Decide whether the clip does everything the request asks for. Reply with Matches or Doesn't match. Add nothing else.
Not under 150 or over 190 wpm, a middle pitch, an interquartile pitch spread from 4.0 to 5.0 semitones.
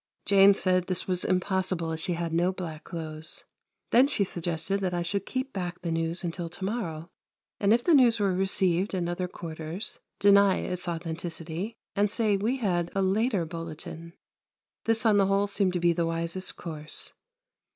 Doesn't match